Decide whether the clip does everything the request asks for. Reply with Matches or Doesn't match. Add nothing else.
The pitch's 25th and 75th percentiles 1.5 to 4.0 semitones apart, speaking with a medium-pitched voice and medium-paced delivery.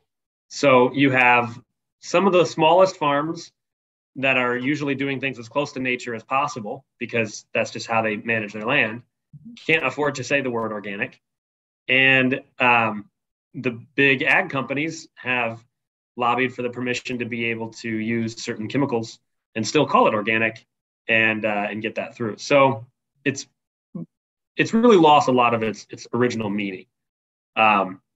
Doesn't match